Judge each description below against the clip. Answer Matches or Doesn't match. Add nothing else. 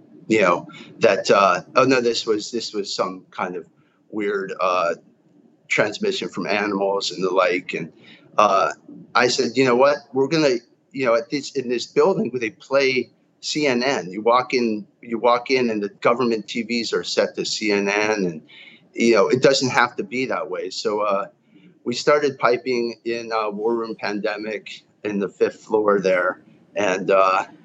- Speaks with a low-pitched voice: Matches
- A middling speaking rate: Matches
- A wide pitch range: Doesn't match